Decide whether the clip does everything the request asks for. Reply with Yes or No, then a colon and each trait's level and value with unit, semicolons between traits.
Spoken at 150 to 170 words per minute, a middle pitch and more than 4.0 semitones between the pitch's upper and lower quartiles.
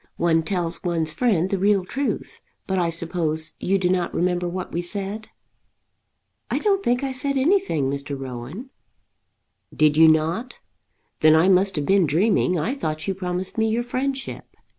Yes: average, 165 wpm; medium, 180 Hz; wide, 5.5 semitones